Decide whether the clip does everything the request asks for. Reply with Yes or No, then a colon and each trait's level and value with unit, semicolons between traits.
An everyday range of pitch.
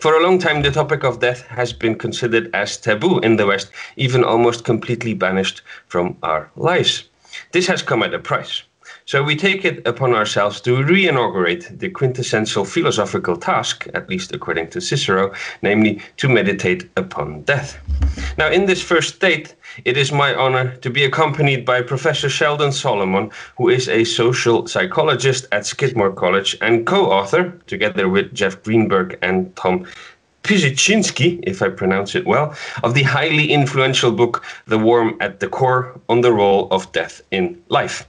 No: wide, 5.7 semitones